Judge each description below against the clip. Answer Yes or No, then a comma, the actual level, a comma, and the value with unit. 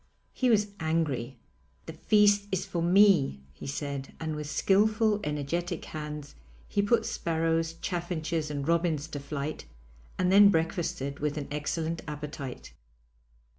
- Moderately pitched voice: Yes, medium, 160 Hz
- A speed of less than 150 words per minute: Yes, slow, 135 wpm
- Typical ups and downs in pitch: Yes, average, 3.8 semitones